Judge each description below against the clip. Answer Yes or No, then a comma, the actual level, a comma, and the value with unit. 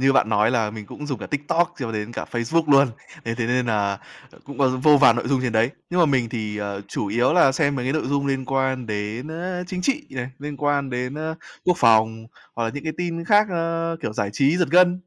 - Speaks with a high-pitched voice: No, low, 135 Hz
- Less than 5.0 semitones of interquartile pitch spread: No, wide, 5.5 semitones